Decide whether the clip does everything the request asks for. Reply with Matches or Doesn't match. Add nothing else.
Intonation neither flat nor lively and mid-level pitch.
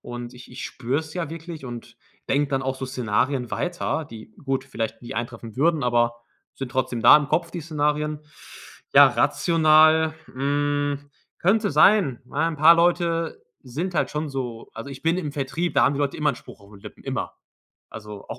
Matches